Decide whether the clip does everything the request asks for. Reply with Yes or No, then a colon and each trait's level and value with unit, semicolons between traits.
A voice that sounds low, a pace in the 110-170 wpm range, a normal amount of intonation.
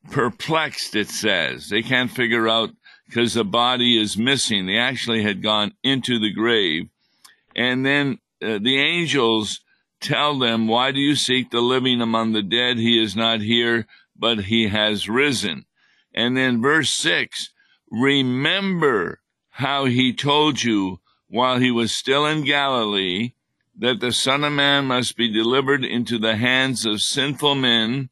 Yes: low, 120 Hz; average, 155 wpm; average, 3.1 semitones